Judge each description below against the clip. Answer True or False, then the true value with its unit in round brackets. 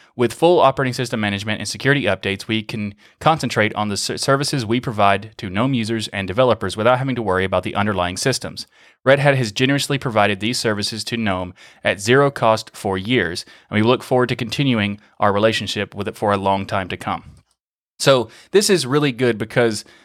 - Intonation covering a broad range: False (4.0 semitones)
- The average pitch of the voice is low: True (110 Hz)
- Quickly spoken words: False (195 wpm)